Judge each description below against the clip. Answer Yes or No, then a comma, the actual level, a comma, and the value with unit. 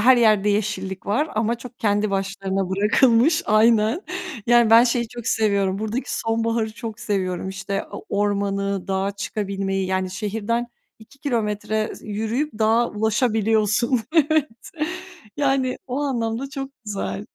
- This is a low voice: No, high, 220 Hz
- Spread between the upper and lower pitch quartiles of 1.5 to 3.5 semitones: Yes, average, 3.0 semitones